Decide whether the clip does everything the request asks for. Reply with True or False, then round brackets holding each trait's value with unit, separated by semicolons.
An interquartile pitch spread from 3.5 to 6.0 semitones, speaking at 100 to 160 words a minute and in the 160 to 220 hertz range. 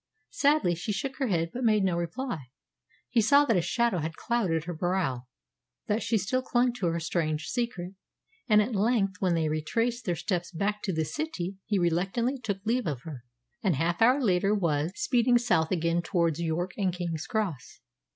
False (5.6 semitones; 190 wpm; 185 Hz)